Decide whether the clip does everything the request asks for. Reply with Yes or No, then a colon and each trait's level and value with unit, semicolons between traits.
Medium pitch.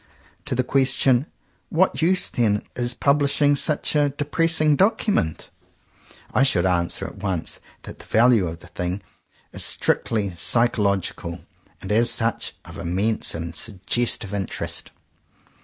No: low, 115 Hz